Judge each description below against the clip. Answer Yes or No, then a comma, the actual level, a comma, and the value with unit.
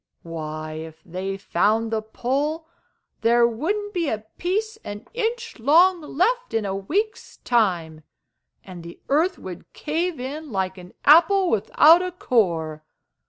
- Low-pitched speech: No, high, 240 Hz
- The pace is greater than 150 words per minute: No, average, 140 wpm